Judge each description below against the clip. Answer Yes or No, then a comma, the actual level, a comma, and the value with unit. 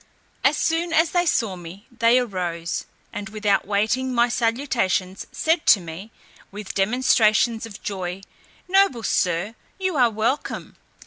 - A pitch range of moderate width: Yes, average, 4.7 semitones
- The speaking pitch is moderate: No, high, 220 Hz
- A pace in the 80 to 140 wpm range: Yes, slow, 135 wpm